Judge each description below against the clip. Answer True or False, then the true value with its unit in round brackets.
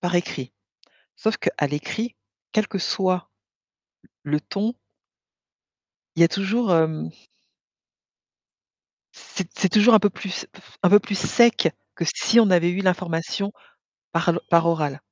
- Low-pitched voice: False (185 Hz)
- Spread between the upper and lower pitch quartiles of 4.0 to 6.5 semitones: False (3.5 semitones)